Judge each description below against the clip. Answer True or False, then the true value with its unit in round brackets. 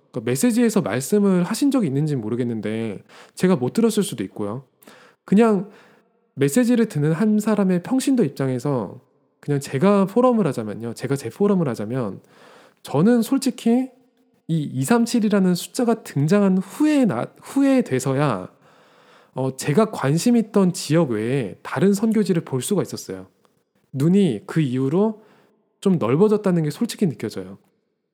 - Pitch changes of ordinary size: False (8.5 semitones)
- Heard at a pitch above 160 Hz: True (190 Hz)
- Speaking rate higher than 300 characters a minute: False (290 characters per minute)